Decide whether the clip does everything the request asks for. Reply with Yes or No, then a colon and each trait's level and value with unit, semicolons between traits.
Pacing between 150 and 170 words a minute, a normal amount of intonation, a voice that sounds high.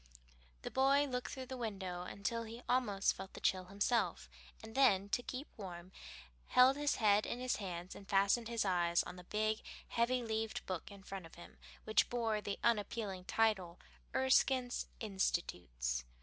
Yes: average, 165 wpm; average, 4.3 semitones; high, 210 Hz